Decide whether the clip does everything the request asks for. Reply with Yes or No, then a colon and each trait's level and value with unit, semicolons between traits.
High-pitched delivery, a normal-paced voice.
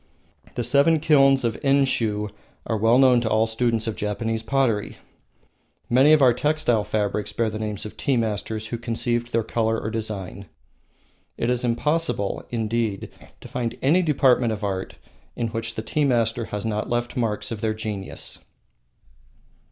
No: low, 115 Hz; average, 160 wpm